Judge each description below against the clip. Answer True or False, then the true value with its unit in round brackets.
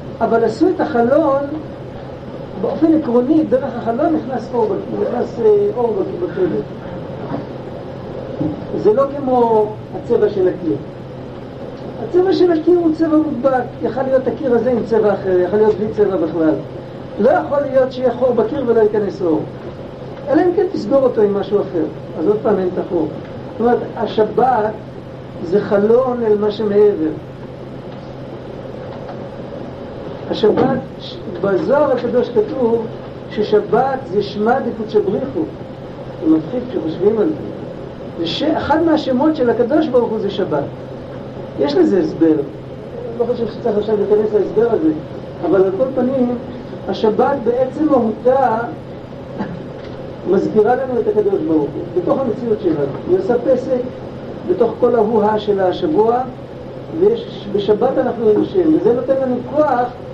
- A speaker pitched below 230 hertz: False (240 Hz)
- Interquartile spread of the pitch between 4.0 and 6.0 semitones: True (5.2 semitones)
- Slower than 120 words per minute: False (135 wpm)